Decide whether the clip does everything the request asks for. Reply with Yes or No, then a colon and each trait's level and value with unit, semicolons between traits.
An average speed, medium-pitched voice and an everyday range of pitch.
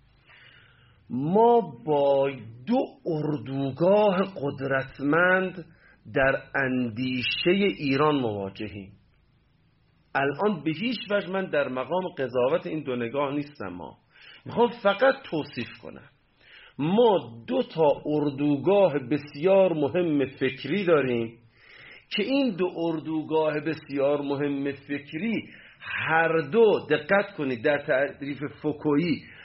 No: slow, 100 wpm; medium, 145 Hz; average, 4.9 semitones